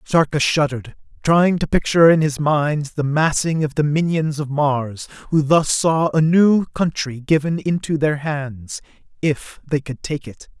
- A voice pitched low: No, medium, 150 Hz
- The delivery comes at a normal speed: Yes, average, 165 wpm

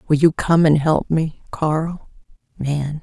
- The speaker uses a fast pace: No, average, 160 wpm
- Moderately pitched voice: Yes, medium, 155 Hz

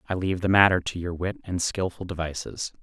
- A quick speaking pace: Yes, fast, 210 wpm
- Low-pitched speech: Yes, very low, 90 Hz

